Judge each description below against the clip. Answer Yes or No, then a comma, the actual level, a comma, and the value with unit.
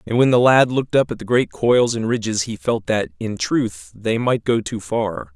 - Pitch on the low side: Yes, low, 110 Hz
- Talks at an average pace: No, fast, 245 wpm